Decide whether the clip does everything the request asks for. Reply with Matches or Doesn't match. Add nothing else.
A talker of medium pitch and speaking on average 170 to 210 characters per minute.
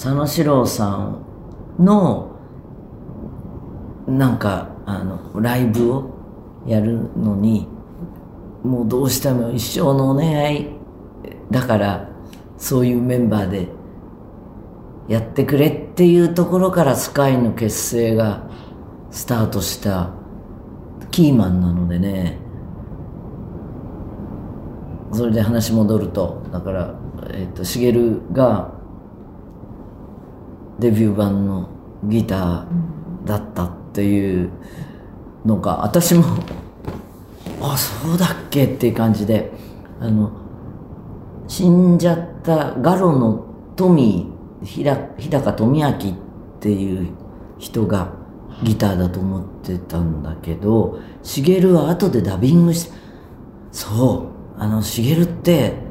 Doesn't match